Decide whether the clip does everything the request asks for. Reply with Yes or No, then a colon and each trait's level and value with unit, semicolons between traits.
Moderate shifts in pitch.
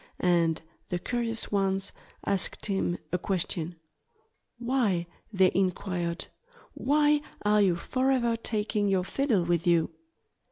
Yes: average, 4.7 semitones